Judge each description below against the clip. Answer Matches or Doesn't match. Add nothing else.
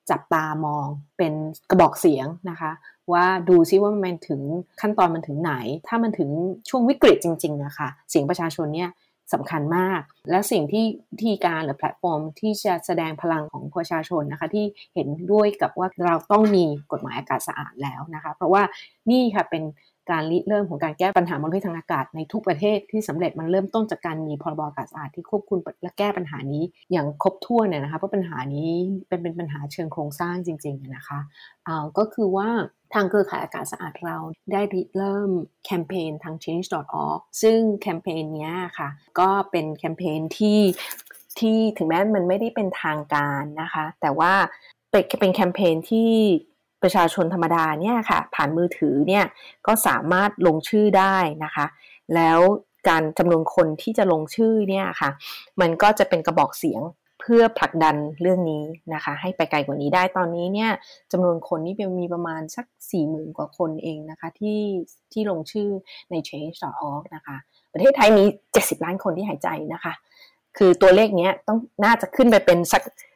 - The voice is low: Doesn't match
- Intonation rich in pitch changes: Doesn't match